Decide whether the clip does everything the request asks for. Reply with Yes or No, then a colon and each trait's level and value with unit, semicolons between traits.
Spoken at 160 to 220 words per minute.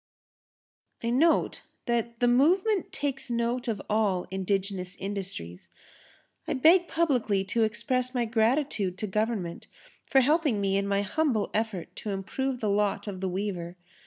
No: average, 145 wpm